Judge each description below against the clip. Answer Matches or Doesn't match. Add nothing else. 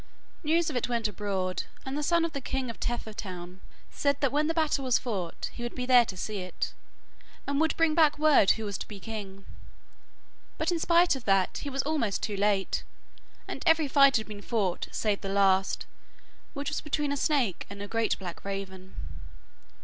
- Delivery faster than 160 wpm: Matches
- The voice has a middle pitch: Doesn't match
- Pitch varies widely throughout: Matches